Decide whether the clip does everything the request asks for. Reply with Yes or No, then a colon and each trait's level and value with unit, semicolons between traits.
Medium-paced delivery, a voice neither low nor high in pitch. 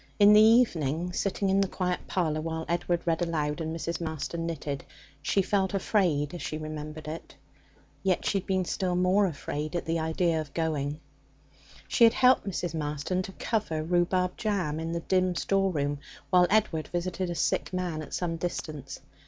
Yes: average, 180 wpm; medium, 170 Hz